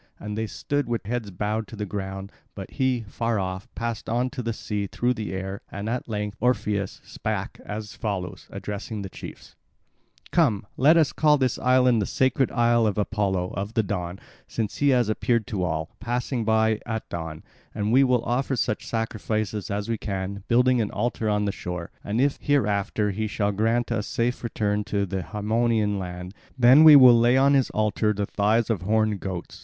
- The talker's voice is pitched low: Yes, low, 110 Hz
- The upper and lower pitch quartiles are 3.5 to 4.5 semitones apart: No, average, 3.0 semitones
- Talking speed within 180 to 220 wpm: Yes, average, 195 wpm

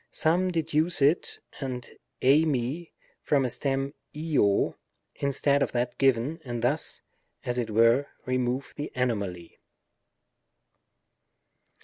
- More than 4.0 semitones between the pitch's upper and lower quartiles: No, average, 3.5 semitones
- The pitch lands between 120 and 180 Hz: Yes, low, 135 Hz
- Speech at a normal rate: No, slow, 110 wpm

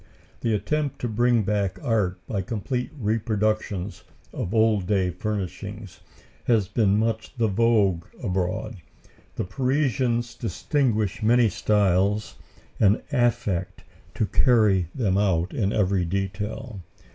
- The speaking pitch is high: No, low, 105 Hz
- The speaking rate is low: Yes, slow, 115 wpm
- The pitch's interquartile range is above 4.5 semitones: No, average, 3.2 semitones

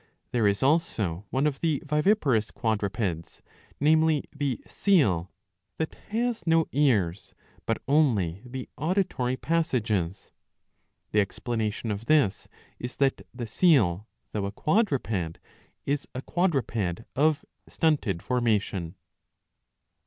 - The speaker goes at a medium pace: No, slow, 110 wpm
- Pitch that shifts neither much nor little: No, wide, 7.1 semitones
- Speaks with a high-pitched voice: No, low, 125 Hz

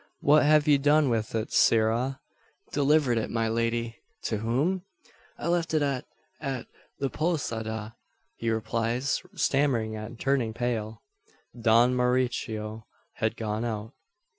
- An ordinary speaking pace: No, slow, 130 wpm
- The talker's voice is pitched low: Yes, low, 120 Hz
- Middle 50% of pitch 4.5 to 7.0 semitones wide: No, average, 3.8 semitones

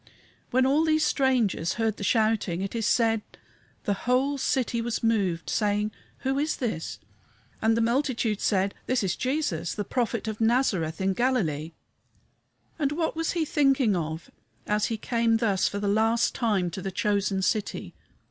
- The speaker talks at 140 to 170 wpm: Yes, average, 165 wpm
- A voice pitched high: Yes, high, 225 Hz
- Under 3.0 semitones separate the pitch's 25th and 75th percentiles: No, average, 4.5 semitones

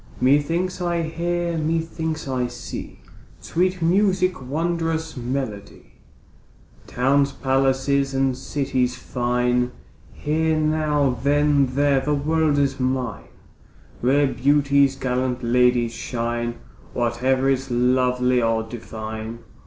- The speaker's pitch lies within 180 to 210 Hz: No, low, 135 Hz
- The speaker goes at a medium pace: No, slow, 100 wpm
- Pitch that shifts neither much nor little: Yes, average, 3.8 semitones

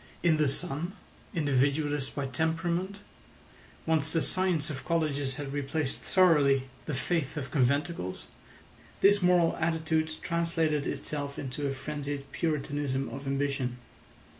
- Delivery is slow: Yes, slow, 120 wpm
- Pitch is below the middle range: No, medium, 150 Hz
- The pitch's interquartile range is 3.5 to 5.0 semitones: No, average, 3.0 semitones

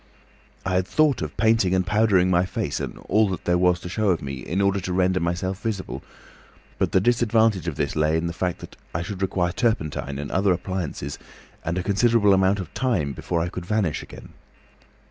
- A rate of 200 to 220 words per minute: Yes, fast, 205 wpm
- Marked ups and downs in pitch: No, average, 3.1 semitones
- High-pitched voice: No, very low, 95 Hz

